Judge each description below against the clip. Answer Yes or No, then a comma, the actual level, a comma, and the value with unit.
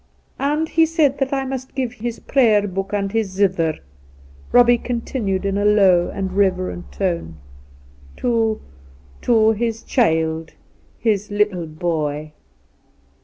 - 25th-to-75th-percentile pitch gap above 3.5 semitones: Yes, wide, 5.6 semitones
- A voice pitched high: Yes, high, 205 Hz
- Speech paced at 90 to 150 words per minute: Yes, average, 145 wpm